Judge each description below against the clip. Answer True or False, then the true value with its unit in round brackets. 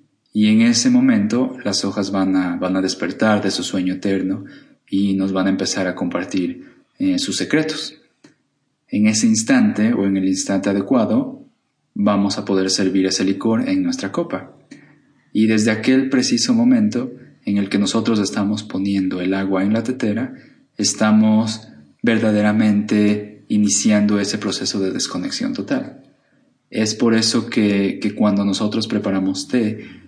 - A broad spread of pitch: True (8.1 semitones)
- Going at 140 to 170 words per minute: True (150 wpm)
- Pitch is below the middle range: True (105 Hz)